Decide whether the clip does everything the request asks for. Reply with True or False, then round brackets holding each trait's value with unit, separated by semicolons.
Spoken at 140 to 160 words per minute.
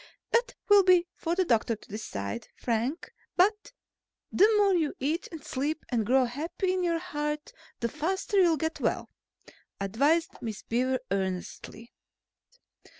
True (145 wpm)